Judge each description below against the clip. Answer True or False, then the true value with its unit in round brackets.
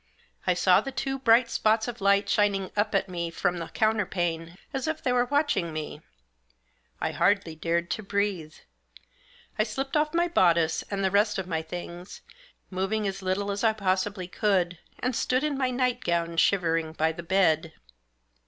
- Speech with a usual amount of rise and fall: True (4.4 semitones)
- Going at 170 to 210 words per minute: True (175 wpm)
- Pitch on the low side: False (195 Hz)